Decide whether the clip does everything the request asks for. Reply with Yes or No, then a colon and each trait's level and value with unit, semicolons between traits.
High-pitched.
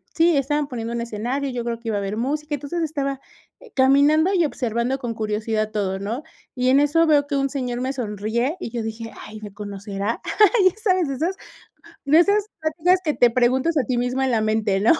Yes: very high, 255 Hz